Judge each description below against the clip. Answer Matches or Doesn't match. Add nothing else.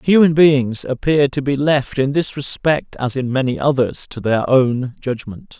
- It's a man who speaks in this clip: Matches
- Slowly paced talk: Doesn't match